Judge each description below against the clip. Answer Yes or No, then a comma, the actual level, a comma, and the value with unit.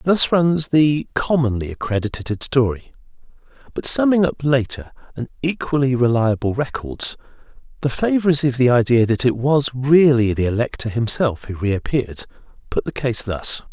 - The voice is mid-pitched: No, low, 130 Hz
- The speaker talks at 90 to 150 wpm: Yes, average, 140 wpm